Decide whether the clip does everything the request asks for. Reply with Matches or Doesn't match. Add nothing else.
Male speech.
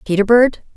Doesn't match